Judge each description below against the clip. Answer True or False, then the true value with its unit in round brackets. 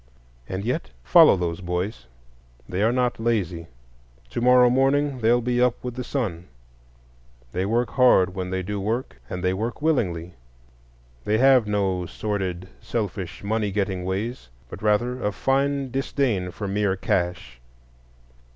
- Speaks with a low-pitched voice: True (105 Hz)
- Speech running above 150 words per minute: False (145 wpm)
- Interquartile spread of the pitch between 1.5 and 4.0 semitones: False (5.0 semitones)